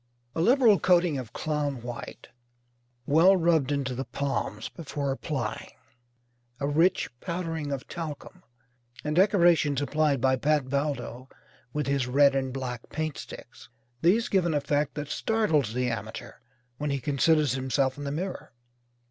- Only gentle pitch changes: No, average, 3.5 semitones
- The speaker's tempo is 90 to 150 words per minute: Yes, average, 145 wpm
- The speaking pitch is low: No, medium, 145 Hz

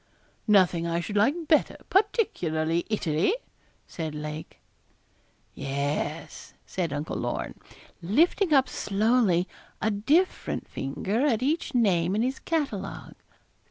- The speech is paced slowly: Yes, slow, 110 wpm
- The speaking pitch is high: Yes, high, 200 Hz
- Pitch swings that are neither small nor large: No, wide, 8.5 semitones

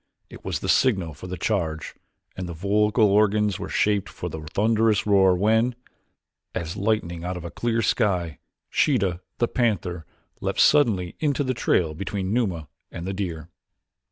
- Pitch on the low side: Yes, low, 100 Hz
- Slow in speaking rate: No, average, 160 wpm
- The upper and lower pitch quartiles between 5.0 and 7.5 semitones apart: No, average, 3.9 semitones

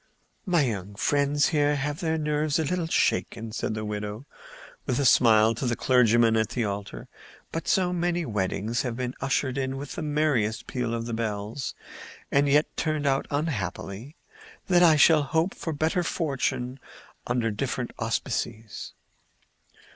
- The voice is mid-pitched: No, low, 130 Hz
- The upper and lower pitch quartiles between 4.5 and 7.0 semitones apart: Yes, average, 5.0 semitones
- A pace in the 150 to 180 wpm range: Yes, average, 160 wpm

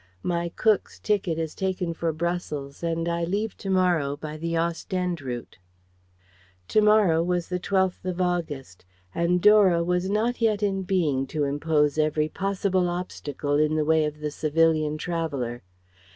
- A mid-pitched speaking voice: Yes, medium, 170 Hz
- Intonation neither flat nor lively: Yes, average, 3.3 semitones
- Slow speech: No, average, 155 wpm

